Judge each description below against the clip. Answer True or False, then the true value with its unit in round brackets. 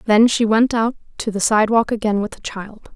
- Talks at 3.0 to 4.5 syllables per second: False (5.0 syllables/s)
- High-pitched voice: True (220 Hz)